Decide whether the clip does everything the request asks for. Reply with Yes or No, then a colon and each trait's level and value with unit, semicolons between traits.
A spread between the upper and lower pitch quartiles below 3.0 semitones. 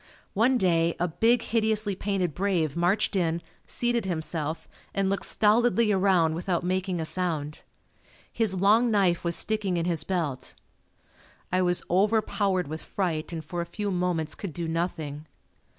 No: average, 3.5 semitones